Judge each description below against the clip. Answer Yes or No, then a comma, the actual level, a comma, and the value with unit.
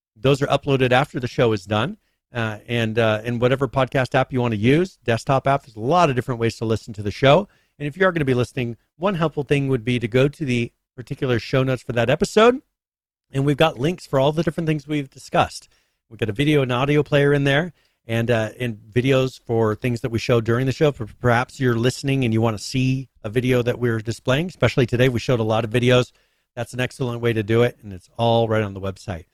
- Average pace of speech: No, fast, 250 wpm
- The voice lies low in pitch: Yes, low, 125 Hz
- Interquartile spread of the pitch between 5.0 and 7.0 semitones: No, average, 3.4 semitones